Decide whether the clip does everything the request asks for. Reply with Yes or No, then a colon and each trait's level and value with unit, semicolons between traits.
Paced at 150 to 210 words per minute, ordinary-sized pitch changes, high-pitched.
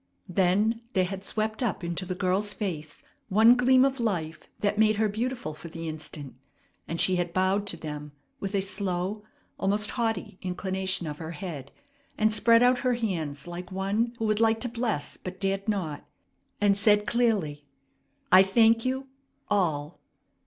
Yes: average, 165 wpm; average, 4.0 semitones; high, 195 Hz